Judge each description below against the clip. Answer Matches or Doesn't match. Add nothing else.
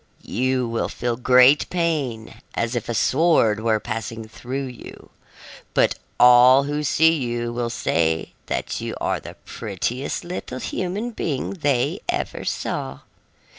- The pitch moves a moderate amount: Matches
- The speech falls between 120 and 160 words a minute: Matches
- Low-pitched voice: Matches